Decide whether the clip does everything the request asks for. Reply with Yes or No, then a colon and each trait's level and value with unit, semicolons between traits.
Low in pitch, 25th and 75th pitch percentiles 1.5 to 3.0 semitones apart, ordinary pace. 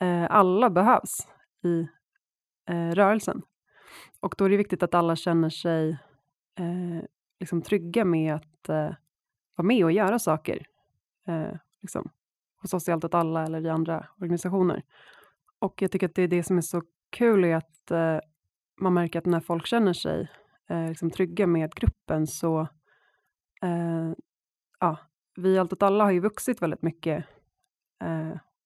No: medium, 170 Hz; narrow, 2.6 semitones; average, 160 wpm